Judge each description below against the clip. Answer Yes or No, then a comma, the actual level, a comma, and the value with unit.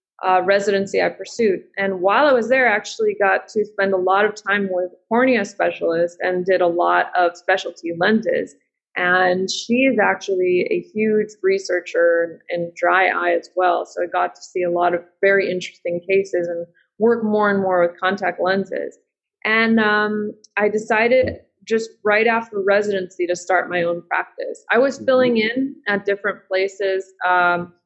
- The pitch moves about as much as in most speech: Yes, average, 3.5 semitones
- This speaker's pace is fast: No, average, 175 wpm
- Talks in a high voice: Yes, high, 195 Hz